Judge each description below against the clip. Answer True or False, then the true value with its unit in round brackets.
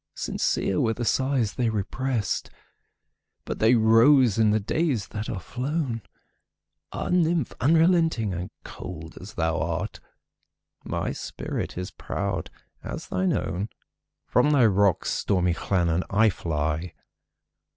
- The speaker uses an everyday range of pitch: False (6.0 semitones)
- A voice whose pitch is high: False (110 Hz)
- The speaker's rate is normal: False (110 wpm)